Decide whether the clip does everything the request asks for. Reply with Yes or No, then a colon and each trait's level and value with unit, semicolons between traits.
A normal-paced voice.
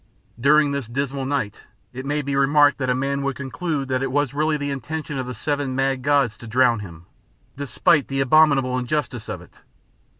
Yes: average, 195 wpm